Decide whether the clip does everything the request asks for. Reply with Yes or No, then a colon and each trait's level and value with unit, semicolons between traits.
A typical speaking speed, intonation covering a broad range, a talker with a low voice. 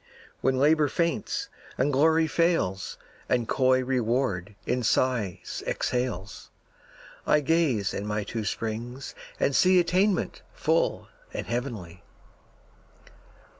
No: slow, 105 wpm; wide, 6.3 semitones; low, 130 Hz